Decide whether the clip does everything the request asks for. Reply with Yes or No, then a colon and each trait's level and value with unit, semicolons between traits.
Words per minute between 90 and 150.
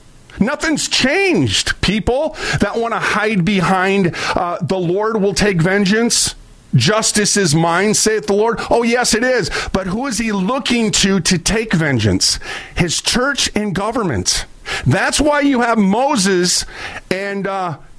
Yes: average, 145 wpm